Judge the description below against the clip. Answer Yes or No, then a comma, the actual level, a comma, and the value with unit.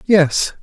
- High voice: No, medium, 180 Hz